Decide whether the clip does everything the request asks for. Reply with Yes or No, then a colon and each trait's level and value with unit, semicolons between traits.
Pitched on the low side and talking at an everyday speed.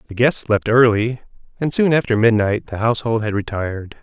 Yes: low, 115 Hz; average, 180 wpm